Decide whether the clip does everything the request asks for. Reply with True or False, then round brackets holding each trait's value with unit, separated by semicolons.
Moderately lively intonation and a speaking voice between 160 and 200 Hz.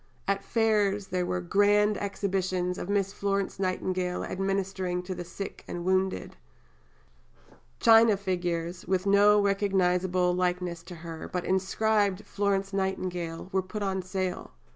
False (1.8 semitones; 190 Hz)